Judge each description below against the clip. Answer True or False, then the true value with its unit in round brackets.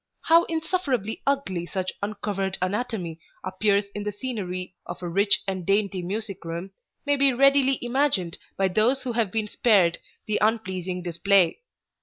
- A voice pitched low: False (200 Hz)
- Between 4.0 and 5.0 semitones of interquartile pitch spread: True (4.6 semitones)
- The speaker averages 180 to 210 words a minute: False (150 wpm)